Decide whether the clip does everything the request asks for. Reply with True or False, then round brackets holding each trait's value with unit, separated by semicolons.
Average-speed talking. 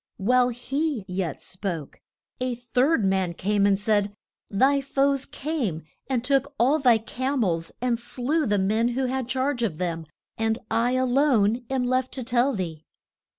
True (165 wpm)